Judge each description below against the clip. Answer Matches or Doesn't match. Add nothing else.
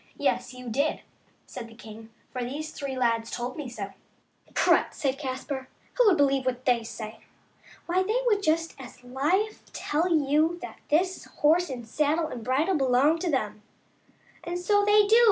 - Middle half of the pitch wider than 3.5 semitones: Matches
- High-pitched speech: Matches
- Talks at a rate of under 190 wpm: Matches